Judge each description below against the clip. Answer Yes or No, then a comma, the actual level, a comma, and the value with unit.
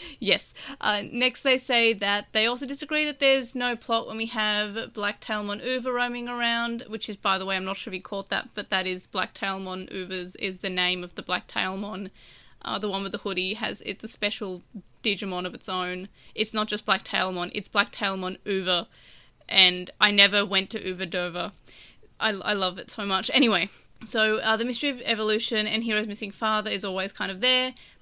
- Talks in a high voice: Yes, high, 210 Hz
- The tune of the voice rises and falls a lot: No, average, 3.0 semitones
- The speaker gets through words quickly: Yes, fast, 210 wpm